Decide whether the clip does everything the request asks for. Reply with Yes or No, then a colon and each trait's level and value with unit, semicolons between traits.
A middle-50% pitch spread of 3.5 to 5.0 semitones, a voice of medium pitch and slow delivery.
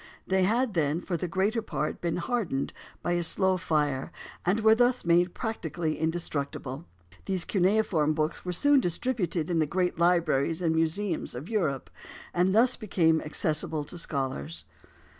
No: average, 3.8 semitones; medium, 175 Hz; average, 155 wpm